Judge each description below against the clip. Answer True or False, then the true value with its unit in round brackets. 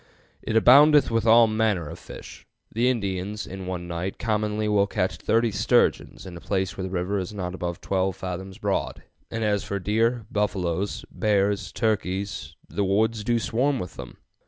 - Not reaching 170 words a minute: False (175 wpm)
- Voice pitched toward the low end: True (100 Hz)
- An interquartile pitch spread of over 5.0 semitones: False (3.1 semitones)